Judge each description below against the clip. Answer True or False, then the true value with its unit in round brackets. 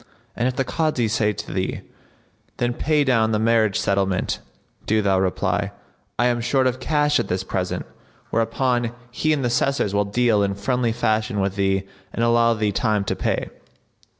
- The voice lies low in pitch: True (115 Hz)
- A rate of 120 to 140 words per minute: False (180 wpm)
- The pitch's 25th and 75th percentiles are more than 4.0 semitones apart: False (3.6 semitones)